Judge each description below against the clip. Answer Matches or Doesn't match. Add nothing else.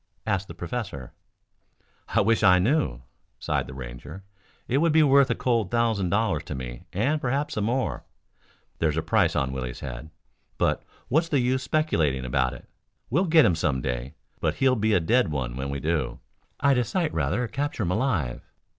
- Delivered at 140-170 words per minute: Doesn't match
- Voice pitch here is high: Doesn't match